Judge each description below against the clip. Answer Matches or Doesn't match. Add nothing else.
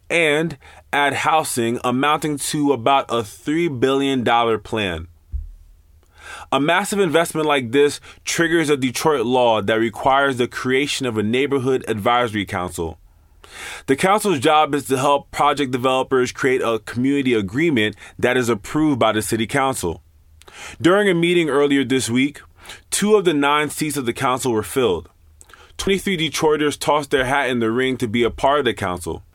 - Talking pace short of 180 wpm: Matches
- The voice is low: Matches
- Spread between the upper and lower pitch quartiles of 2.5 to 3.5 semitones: Doesn't match